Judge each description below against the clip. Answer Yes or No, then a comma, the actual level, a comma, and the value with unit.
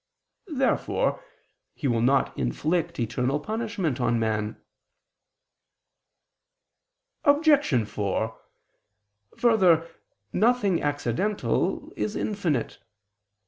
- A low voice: No, medium, 160 Hz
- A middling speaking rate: No, slow, 70 wpm